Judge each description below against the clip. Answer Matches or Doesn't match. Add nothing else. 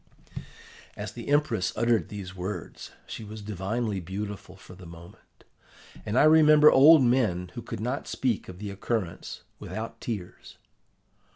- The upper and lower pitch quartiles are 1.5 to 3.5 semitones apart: Doesn't match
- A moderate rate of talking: Matches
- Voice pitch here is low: Matches